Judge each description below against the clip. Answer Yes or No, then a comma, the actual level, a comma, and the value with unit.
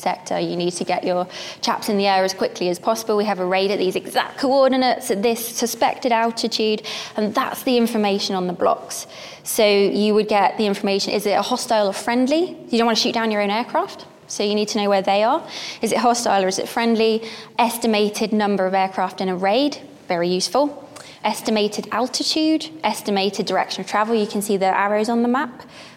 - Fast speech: Yes, fast, 215 wpm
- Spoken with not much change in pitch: No, average, 3.1 semitones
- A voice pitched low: No, high, 215 Hz